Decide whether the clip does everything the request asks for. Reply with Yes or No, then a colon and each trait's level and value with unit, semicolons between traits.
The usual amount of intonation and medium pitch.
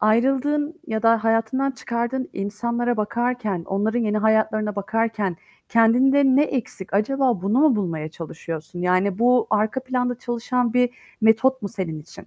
No: average, 3.3 semitones; high, 225 Hz